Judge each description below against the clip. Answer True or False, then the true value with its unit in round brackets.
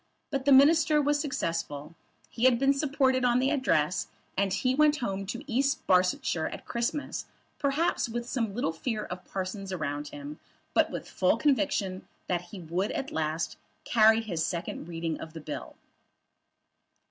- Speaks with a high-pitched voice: True (220 Hz)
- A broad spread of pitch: True (8.0 semitones)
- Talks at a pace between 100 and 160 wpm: False (170 wpm)